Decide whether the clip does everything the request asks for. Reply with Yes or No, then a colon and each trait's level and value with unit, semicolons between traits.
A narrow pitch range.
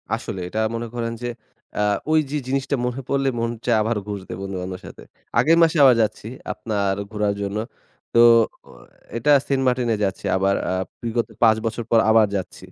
No: average, 4.0 semitones